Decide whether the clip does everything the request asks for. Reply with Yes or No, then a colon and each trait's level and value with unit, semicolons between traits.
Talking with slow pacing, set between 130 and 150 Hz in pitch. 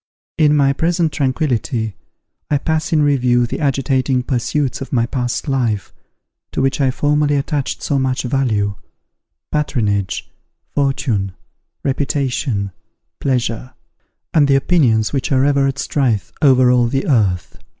Yes: slow, 130 wpm; low, 135 Hz